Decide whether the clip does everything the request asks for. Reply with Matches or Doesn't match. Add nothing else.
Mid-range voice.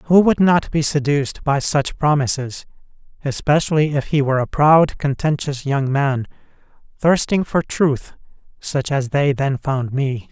Matches